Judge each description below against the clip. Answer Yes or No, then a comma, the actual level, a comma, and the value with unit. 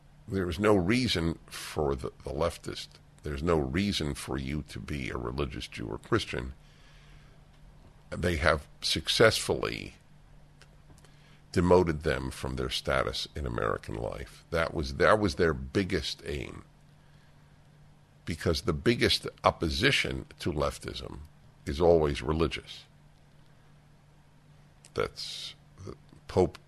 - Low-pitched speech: Yes, very low, 80 Hz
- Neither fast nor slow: No, slow, 110 wpm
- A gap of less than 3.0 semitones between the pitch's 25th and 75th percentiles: No, average, 4.8 semitones